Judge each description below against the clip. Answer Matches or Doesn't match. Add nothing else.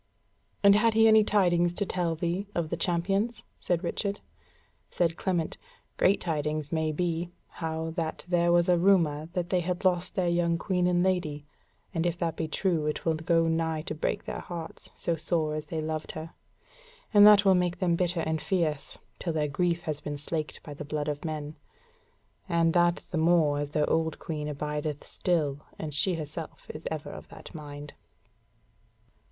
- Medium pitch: Matches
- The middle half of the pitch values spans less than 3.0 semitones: Matches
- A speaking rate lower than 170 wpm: Doesn't match